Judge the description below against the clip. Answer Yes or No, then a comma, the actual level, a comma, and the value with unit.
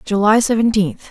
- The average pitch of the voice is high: Yes, high, 215 Hz